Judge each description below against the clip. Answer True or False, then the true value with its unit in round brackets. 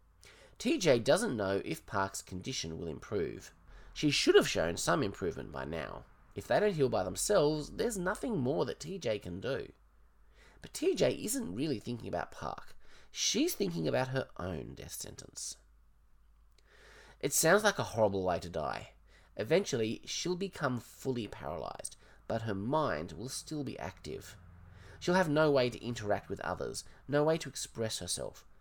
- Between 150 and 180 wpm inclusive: True (160 wpm)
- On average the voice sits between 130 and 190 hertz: False (120 Hz)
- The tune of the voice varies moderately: False (8.1 semitones)